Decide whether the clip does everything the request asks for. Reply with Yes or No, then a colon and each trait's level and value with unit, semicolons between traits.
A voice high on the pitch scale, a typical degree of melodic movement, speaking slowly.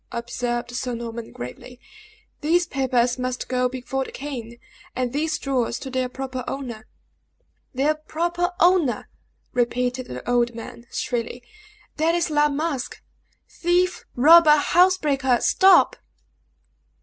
Yes: very high, 260 Hz; average, 4.1 semitones; slow, 120 wpm